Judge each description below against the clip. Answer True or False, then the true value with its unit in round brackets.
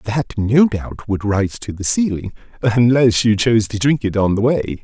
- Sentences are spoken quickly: True (210 wpm)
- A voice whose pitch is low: True (110 Hz)